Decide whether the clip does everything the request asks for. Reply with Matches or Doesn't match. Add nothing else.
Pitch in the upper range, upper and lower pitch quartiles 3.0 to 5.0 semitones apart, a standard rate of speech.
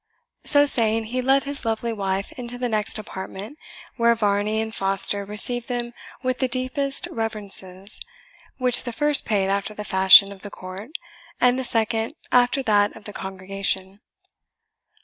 Matches